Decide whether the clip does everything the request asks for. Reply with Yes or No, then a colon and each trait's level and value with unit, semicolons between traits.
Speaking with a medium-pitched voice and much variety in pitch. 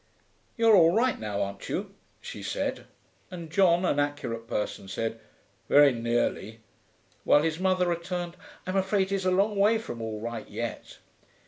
Yes: medium, 165 Hz; wide, 8.5 semitones